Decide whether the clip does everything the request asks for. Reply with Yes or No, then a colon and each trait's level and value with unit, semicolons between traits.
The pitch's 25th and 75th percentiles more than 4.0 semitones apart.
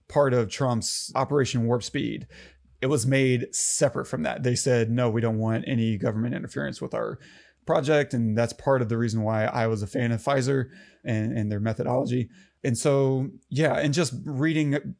No: average, 3.4 semitones